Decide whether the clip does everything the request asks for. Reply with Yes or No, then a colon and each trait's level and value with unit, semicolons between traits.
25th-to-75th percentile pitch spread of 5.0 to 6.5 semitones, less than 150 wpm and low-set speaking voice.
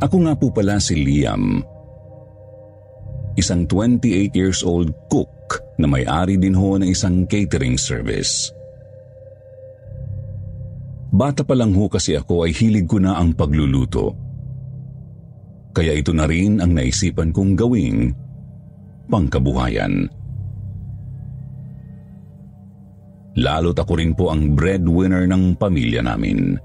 Yes: average, 5.3 semitones; slow, 110 wpm; low, 100 Hz